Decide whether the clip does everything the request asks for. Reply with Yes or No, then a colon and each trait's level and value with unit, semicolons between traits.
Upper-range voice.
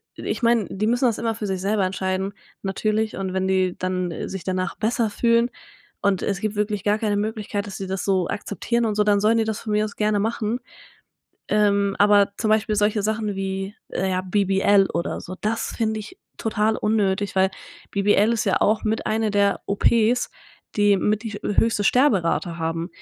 Yes: high, 205 Hz